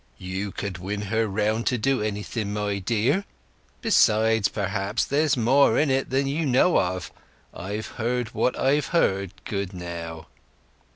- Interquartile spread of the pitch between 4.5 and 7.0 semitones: Yes, average, 4.8 semitones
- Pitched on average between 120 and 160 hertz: No, low, 110 Hz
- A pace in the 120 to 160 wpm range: Yes, average, 150 wpm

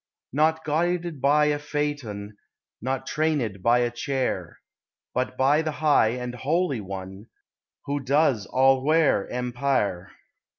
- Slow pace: Yes, slow, 125 wpm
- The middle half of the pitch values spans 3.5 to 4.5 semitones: Yes, average, 4.0 semitones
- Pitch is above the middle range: No, low, 135 Hz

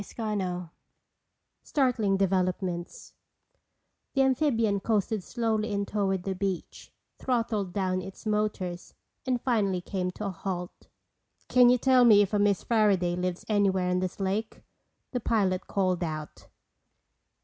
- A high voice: Yes, high, 200 Hz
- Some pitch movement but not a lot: Yes, average, 3.1 semitones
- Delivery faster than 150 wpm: No, slow, 135 wpm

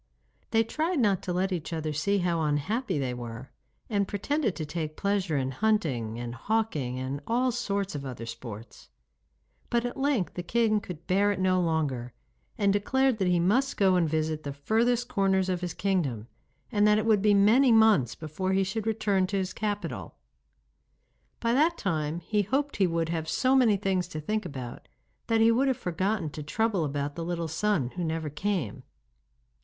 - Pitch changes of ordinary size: No, wide, 5.8 semitones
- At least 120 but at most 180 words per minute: No, average, 190 wpm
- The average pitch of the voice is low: No, high, 190 Hz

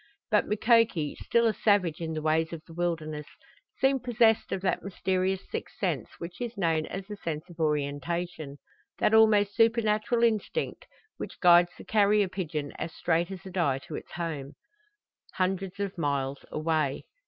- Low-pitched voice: No, medium, 180 Hz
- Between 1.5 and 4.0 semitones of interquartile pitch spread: No, average, 4.8 semitones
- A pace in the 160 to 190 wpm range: Yes, average, 165 wpm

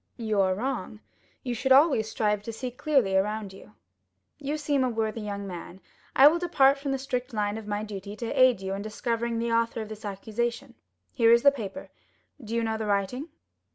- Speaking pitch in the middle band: No, high, 225 Hz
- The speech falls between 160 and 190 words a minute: No, fast, 205 wpm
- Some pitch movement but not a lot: Yes, average, 3.8 semitones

